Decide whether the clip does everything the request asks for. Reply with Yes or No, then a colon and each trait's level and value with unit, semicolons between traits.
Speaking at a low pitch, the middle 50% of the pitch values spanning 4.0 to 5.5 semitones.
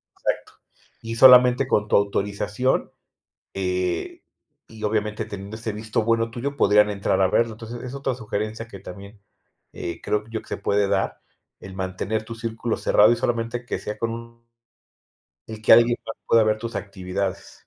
No: low, 110 Hz; narrow, 2.4 semitones